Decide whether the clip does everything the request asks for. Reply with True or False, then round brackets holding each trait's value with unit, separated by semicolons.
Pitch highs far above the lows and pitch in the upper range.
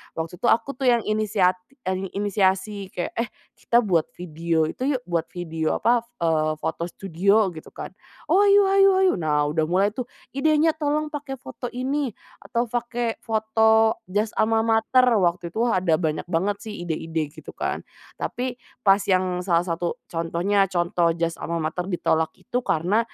True (5.7 semitones; 195 Hz)